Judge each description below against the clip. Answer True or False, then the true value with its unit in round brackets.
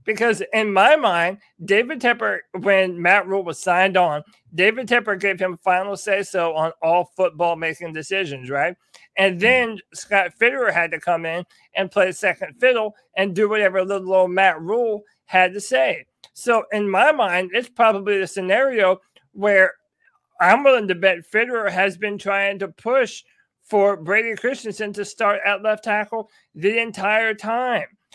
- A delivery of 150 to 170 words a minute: True (165 wpm)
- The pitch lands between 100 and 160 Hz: False (200 Hz)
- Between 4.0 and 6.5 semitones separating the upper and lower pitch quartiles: False (2.9 semitones)